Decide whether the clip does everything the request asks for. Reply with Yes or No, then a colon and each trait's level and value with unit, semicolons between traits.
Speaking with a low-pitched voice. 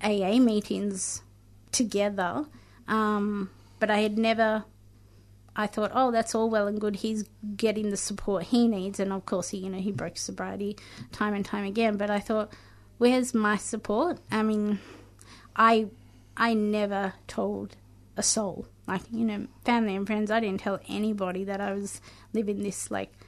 No: high, 205 Hz